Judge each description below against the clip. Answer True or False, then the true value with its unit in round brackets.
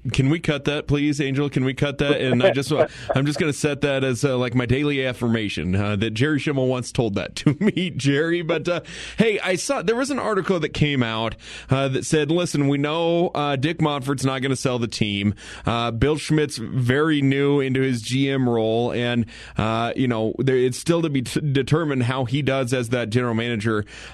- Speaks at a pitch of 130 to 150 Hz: True (135 Hz)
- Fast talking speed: True (220 wpm)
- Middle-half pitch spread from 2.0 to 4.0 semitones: True (3.5 semitones)